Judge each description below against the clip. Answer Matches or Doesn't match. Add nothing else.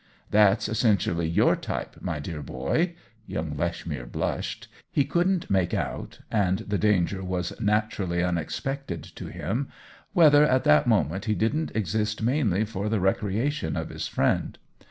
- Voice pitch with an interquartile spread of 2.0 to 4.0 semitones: Doesn't match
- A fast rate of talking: Doesn't match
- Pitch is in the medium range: Doesn't match